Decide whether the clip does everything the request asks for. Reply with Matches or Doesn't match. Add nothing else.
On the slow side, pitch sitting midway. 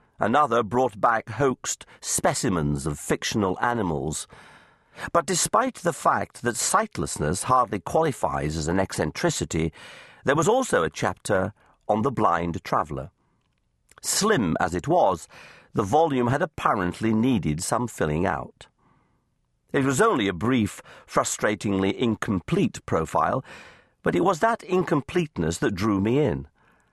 Doesn't match